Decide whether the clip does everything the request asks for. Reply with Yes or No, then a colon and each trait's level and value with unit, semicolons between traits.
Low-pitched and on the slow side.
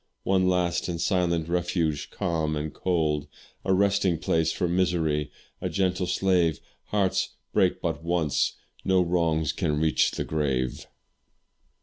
Yes: very low, 85 Hz; slow, 125 wpm